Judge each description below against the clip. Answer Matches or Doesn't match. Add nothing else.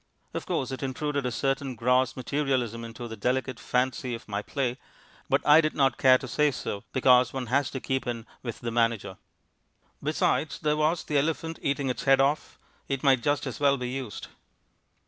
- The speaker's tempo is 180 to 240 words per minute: Matches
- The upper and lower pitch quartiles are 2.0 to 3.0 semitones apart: Matches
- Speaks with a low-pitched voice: Matches